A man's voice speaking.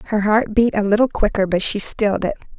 No: female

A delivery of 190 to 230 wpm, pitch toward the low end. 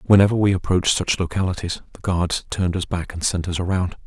Yes: fast, 205 wpm; very low, 90 Hz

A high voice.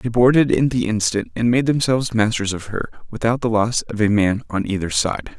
No: low, 115 Hz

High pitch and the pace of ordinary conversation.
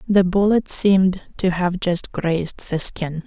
No: medium, 180 Hz; average, 165 wpm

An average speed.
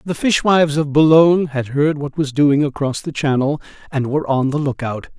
Yes: average, 195 wpm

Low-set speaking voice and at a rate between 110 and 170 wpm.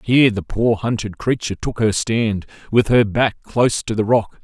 No: low, 110 Hz; fast, 205 wpm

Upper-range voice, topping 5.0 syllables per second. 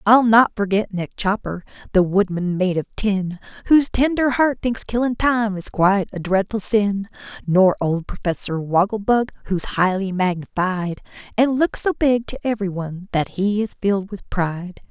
No: high, 200 Hz; 4.6 syllables/s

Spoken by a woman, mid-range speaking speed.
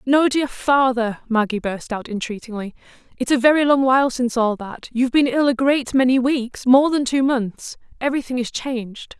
Yes: female; average, 185 wpm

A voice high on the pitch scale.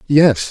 No: low, 130 Hz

